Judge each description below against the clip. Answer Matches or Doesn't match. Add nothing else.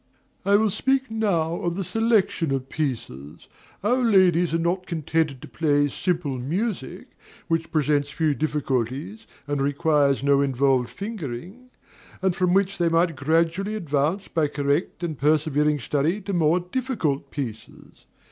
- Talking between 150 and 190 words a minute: Doesn't match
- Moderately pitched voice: Matches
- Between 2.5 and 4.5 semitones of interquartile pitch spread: Doesn't match